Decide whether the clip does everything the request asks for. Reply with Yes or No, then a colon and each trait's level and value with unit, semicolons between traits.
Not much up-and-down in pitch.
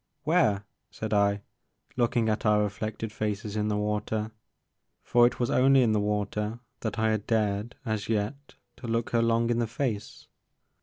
Yes: narrow, 2.1 semitones